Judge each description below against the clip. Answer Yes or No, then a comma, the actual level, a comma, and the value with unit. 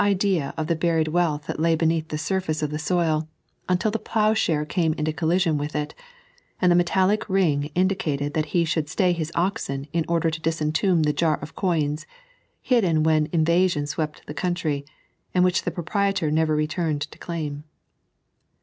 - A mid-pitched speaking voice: Yes, medium, 160 Hz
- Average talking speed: Yes, average, 180 wpm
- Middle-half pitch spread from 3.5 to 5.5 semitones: No, average, 2.8 semitones